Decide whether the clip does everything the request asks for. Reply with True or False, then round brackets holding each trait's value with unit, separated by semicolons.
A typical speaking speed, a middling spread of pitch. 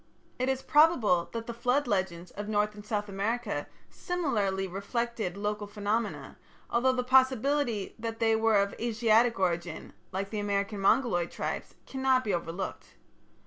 True (145 wpm; 3.5 semitones)